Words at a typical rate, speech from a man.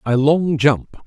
Yes: average, 170 wpm; male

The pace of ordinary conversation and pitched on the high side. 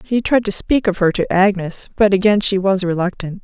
No: fast, 225 wpm; high, 195 Hz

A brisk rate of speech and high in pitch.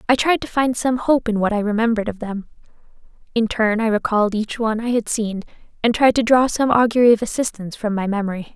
Yes: fast, 225 wpm; high, 225 Hz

